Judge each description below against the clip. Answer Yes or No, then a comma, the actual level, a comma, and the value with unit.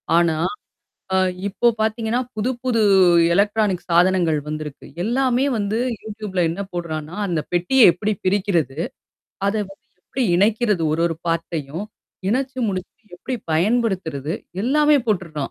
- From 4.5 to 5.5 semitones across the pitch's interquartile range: Yes, average, 4.9 semitones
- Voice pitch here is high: Yes, high, 195 Hz